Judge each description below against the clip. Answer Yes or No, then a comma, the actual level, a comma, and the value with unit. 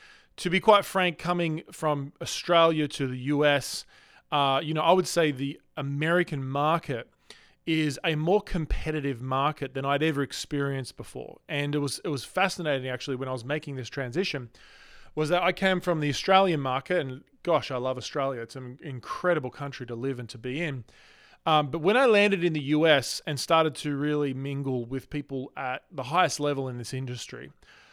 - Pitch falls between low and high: Yes, medium, 145 Hz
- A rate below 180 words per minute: No, average, 185 wpm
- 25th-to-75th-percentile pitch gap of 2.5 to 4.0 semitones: Yes, average, 3.7 semitones